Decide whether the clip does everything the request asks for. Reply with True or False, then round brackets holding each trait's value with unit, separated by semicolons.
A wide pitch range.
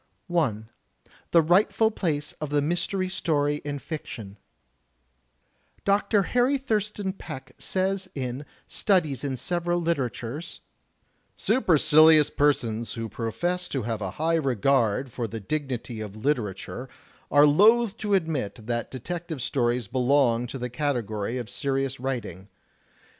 True (6.2 semitones)